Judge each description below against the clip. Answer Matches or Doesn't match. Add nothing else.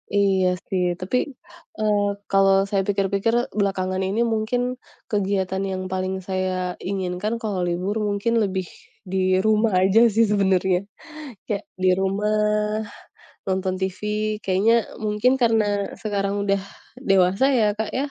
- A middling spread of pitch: Doesn't match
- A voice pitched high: Matches